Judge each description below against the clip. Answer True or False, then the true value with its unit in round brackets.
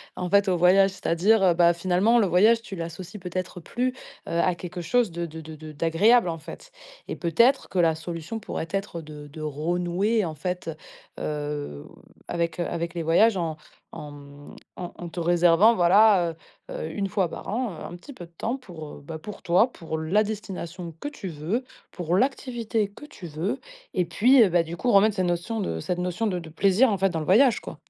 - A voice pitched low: False (180 Hz)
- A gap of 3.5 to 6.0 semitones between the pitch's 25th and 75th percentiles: True (4.1 semitones)